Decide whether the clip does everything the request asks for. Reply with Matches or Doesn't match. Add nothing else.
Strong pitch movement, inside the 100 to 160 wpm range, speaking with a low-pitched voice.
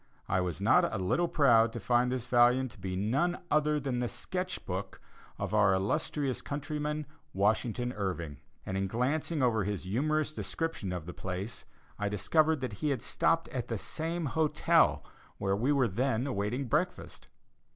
Doesn't match